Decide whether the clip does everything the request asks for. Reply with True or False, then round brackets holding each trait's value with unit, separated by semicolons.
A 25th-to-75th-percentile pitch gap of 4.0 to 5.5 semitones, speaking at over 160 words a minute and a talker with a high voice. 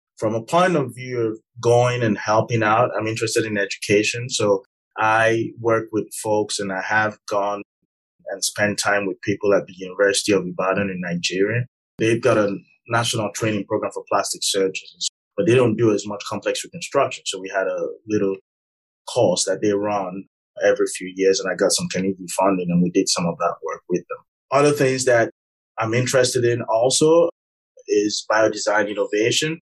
False (4.3 semitones; 180 wpm; 110 Hz)